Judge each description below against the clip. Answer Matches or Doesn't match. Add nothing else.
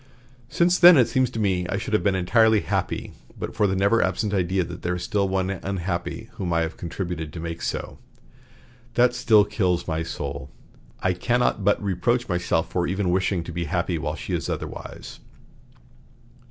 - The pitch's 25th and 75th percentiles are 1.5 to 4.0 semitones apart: Matches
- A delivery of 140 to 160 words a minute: Doesn't match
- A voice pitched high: Doesn't match